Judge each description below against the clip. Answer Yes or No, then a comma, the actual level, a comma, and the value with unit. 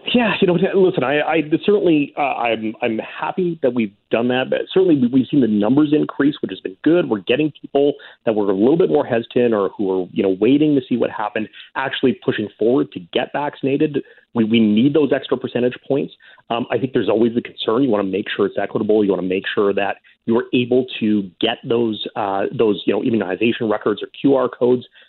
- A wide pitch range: Yes, wide, 6.1 semitones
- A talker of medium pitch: No, low, 125 Hz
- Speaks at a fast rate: Yes, fast, 225 wpm